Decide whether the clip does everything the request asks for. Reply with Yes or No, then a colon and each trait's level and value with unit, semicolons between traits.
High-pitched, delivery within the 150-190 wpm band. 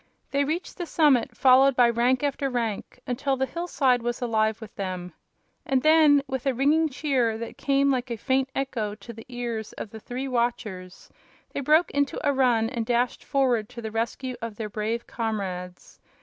Yes: high, 245 Hz; average, 185 wpm